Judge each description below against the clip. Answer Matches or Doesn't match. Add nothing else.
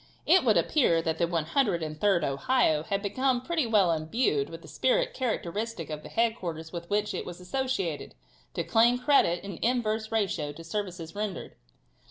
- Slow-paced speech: Doesn't match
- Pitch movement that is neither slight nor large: Doesn't match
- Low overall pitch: Doesn't match